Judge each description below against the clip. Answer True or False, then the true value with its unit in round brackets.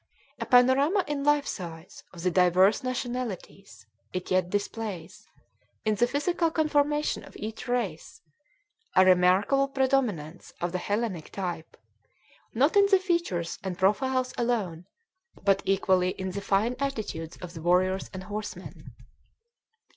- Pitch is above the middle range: True (205 Hz)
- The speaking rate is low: True (130 wpm)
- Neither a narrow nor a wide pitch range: False (6.4 semitones)